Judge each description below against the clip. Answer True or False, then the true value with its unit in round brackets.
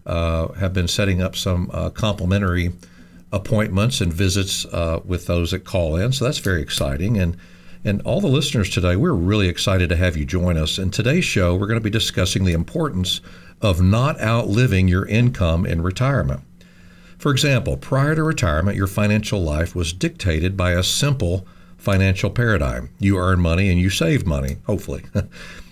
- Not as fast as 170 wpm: False (175 wpm)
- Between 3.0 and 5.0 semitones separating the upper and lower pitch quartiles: True (3.3 semitones)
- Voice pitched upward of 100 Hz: False (95 Hz)